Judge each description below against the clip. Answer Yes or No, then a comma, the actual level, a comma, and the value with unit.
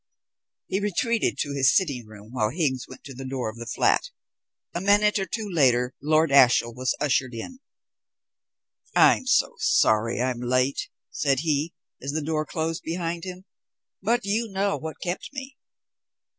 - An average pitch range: No, wide, 6.9 semitones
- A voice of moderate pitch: Yes, medium, 155 Hz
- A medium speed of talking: Yes, average, 160 wpm